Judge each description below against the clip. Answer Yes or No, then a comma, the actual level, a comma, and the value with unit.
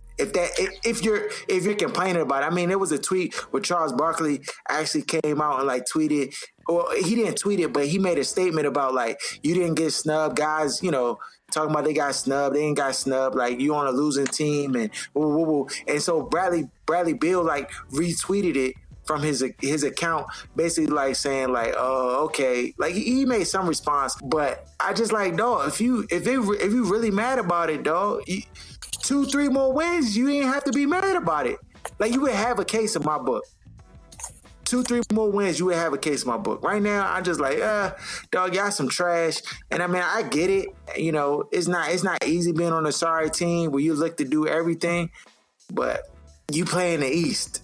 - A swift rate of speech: Yes, fast, 225 wpm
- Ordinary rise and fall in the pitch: No, wide, 6.2 semitones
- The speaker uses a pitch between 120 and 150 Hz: No, medium, 170 Hz